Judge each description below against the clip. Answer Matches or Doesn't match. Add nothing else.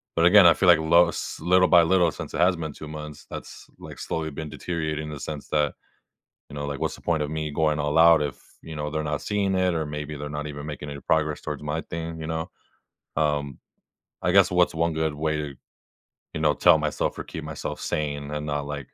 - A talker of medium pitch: Doesn't match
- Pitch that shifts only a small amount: Matches